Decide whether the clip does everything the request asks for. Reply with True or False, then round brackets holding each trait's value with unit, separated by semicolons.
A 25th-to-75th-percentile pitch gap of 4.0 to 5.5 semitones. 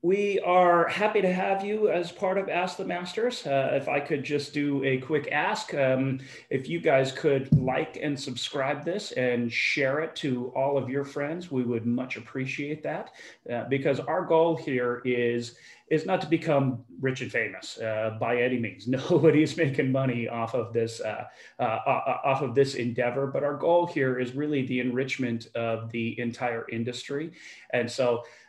True (4.3 semitones)